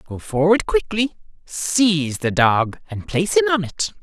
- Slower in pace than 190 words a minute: Yes, average, 165 wpm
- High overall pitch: No, medium, 180 Hz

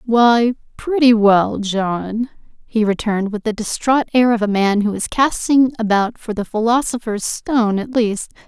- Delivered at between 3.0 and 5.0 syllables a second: Yes, 4.4 syllables/s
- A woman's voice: Yes, female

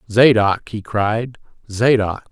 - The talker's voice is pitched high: No, low, 110 Hz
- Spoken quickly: No, slow, 80 wpm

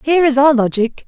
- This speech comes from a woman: Yes, female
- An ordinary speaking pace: No, fast, 225 wpm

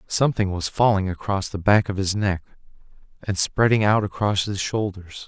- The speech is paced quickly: No, average, 170 wpm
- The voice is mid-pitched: No, low, 100 Hz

